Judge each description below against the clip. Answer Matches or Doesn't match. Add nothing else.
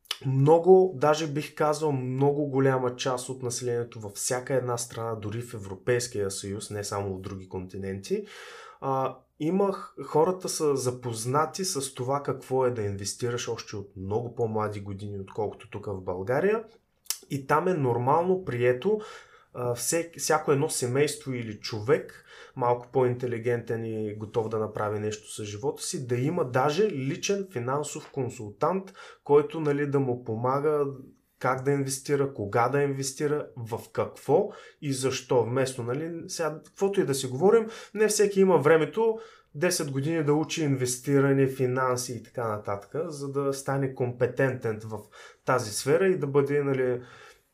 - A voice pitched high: Doesn't match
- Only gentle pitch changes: Doesn't match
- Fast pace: Doesn't match